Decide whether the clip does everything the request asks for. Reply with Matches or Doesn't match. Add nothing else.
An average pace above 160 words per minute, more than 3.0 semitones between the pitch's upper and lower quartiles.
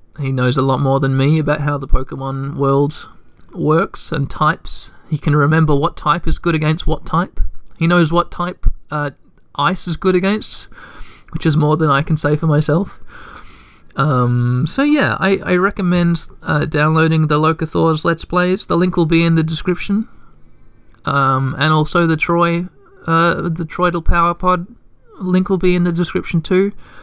Matches